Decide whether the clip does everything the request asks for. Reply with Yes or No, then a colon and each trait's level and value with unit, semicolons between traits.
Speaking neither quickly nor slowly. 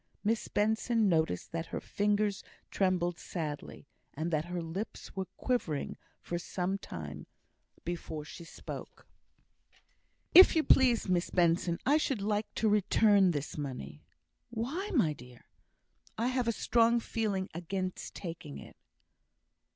No: slow, 130 wpm